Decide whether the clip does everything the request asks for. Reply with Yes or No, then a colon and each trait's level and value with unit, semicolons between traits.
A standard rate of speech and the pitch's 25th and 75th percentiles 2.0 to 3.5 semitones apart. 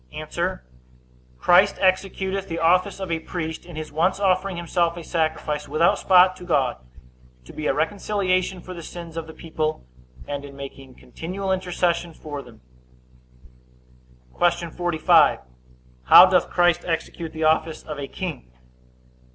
Yes: average, 145 wpm; average, 2.7 semitones